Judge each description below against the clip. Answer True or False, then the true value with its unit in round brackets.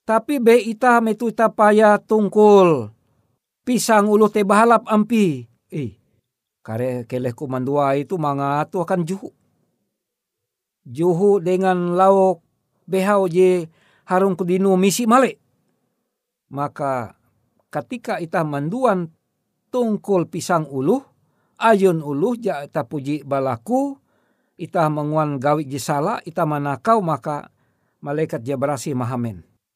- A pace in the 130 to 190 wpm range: False (105 wpm)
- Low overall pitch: False (175 Hz)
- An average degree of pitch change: False (6.7 semitones)